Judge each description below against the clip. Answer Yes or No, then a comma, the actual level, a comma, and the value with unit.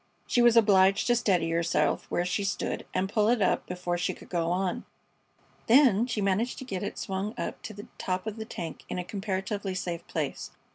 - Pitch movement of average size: Yes, average, 3.3 semitones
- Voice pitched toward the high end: Yes, high, 195 Hz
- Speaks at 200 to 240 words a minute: Yes, fast, 205 wpm